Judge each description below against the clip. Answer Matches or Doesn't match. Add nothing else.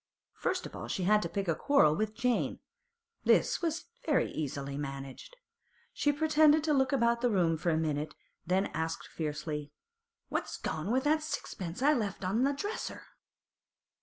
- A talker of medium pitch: Doesn't match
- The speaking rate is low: Doesn't match